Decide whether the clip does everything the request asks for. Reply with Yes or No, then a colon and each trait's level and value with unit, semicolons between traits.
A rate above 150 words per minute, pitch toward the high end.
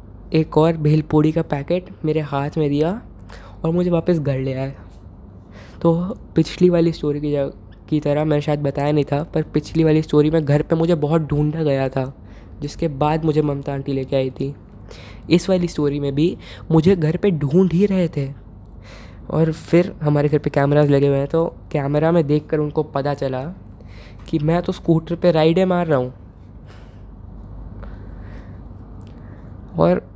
No: average, 175 wpm; medium, 150 Hz